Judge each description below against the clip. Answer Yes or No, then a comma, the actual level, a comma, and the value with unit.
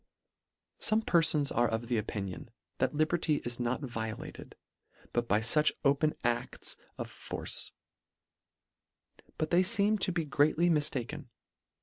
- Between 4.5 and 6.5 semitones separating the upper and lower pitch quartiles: Yes, wide, 5.6 semitones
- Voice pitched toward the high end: No, medium, 145 Hz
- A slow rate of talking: Yes, slow, 125 wpm